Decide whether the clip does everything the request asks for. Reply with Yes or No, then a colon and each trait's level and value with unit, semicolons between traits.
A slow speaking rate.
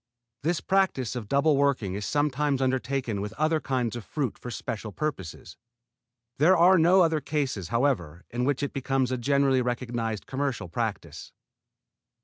No: average, 150 wpm